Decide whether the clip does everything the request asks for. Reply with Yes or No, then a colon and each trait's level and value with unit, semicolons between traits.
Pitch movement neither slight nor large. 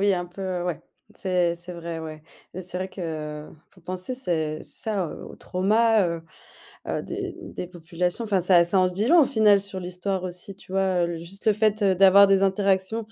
No: narrow, 2.2 semitones